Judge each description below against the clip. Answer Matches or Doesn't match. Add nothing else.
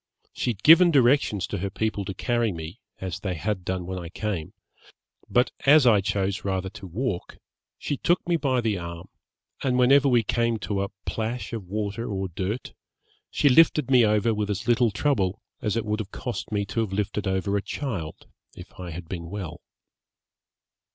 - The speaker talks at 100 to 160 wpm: Doesn't match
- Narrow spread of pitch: Doesn't match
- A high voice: Doesn't match